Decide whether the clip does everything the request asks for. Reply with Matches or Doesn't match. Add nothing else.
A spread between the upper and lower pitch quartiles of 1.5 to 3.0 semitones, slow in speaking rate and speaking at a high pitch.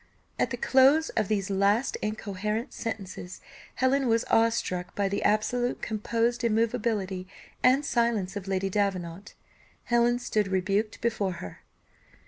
Doesn't match